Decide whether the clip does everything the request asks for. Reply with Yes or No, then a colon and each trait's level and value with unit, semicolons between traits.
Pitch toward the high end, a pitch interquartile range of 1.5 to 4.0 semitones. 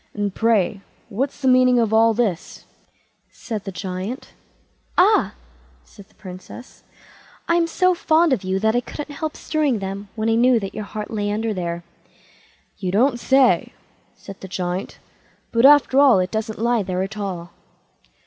No: high, 220 Hz; average, 4.8 semitones